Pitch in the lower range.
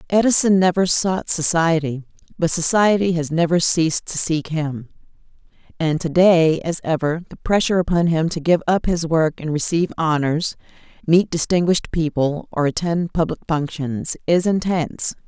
No: medium, 165 Hz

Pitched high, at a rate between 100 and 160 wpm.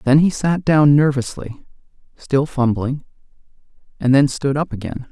No: medium, 140 Hz; average, 140 wpm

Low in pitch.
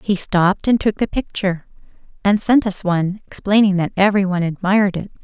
No: high, 195 Hz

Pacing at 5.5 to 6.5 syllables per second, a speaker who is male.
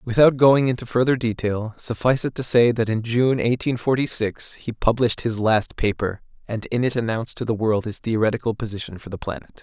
Yes: 5.6 syllables/s; male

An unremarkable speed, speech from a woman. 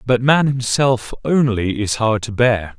No: average, 170 wpm; male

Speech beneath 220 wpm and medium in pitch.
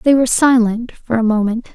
No: fast, 205 wpm; high, 235 Hz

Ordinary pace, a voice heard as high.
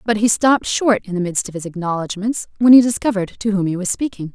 No: fast, 250 wpm; high, 205 Hz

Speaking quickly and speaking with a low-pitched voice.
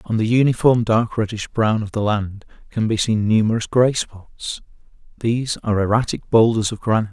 No: average, 175 wpm; low, 110 Hz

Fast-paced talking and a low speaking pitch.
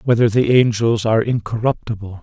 No: slow, 135 wpm; low, 115 Hz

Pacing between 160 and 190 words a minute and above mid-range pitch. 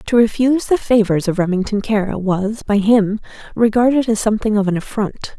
Yes: average, 180 wpm; high, 215 Hz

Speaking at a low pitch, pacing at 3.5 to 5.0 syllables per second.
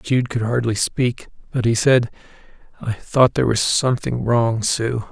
Yes: low, 120 Hz; 4.5 syllables/s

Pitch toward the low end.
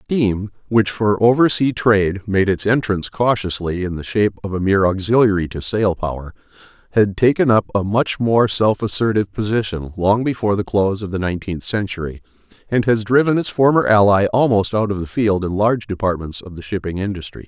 Yes: low, 105 Hz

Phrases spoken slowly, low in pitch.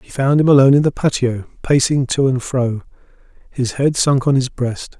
No: fast, 205 wpm; low, 130 Hz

